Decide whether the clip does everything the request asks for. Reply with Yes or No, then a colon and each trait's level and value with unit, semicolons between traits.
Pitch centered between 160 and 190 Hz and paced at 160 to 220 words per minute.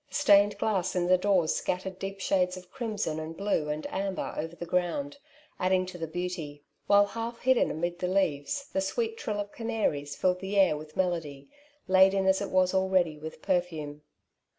Yes: medium, 185 Hz; average, 185 wpm